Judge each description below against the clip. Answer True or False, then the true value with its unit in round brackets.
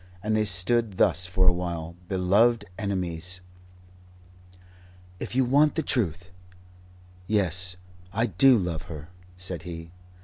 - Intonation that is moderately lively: True (3.7 semitones)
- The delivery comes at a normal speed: False (125 wpm)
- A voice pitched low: True (95 Hz)